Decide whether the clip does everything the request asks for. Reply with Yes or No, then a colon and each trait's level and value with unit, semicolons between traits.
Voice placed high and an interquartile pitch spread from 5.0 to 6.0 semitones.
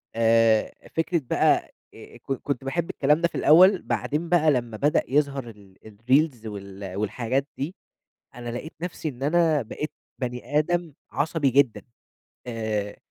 No: low, 135 Hz; wide, 5.4 semitones